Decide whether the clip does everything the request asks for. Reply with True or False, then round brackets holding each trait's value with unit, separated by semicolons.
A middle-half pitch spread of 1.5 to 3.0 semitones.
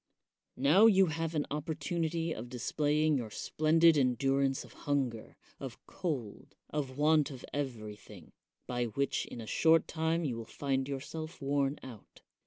False (3.7 semitones)